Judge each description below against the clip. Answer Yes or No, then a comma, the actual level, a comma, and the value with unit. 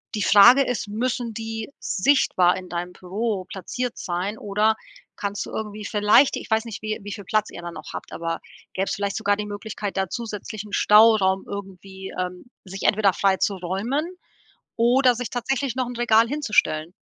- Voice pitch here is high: Yes, high, 210 Hz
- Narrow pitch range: No, average, 3.1 semitones